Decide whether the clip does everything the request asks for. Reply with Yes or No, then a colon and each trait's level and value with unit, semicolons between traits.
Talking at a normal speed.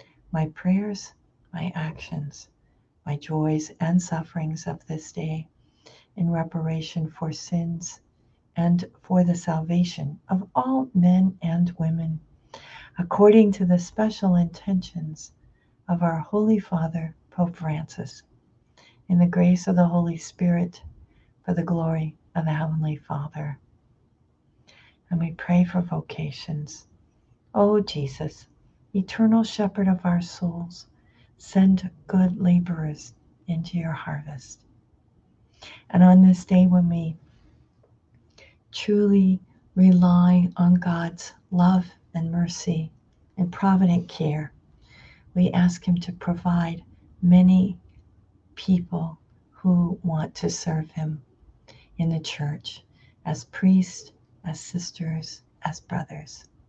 No: slow, 110 wpm